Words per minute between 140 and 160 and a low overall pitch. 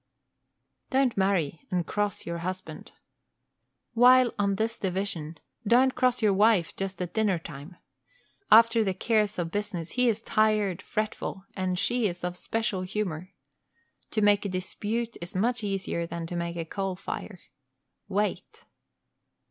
No: average, 145 wpm; high, 200 Hz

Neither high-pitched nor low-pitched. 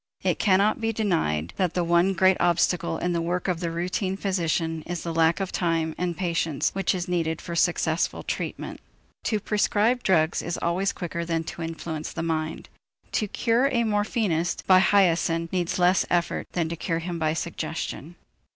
Yes: medium, 175 Hz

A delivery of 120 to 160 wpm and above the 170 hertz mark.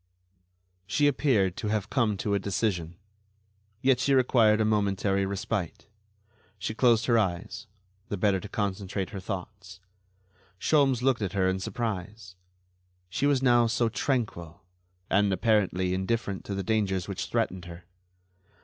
No: average, 140 wpm; low, 100 Hz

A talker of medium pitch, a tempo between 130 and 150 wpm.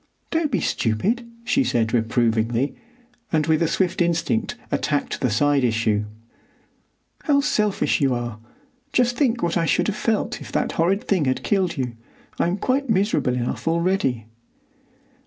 Yes: medium, 165 Hz; average, 145 wpm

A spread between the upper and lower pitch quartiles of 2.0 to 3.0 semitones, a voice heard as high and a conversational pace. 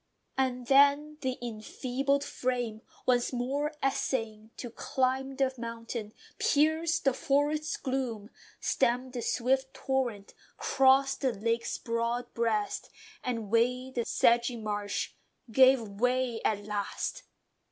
No: average, 2.7 semitones; very high, 250 Hz; slow, 115 wpm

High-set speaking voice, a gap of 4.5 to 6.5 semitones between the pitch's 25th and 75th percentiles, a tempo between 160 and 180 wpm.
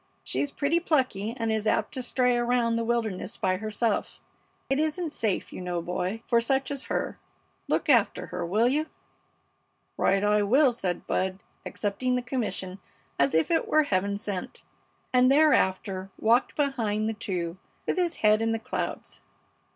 Yes: high, 225 Hz; average, 4.9 semitones; average, 165 wpm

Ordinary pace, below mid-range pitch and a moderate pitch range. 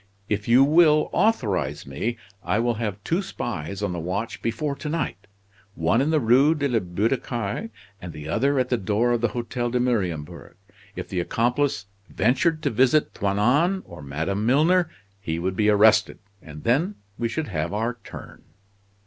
No: average, 180 wpm; low, 115 Hz; wide, 6.0 semitones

